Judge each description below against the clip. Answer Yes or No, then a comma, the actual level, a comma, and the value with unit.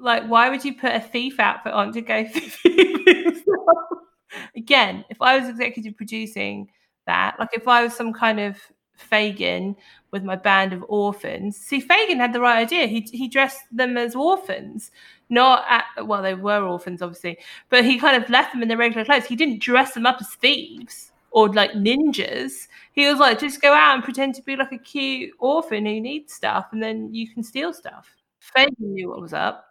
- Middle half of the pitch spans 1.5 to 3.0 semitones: No, average, 4.1 semitones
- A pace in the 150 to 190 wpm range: No, average, 200 wpm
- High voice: Yes, high, 245 Hz